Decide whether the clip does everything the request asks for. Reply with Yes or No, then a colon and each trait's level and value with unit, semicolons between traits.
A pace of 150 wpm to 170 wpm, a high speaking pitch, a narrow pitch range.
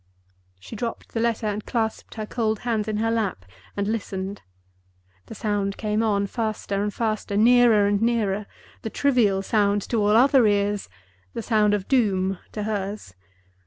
Yes: average, 160 wpm; high, 210 Hz; narrow, 2.0 semitones